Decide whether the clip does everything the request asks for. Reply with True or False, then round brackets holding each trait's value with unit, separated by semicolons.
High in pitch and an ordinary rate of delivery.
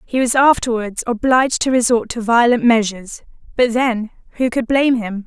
True (235 Hz; 170 wpm)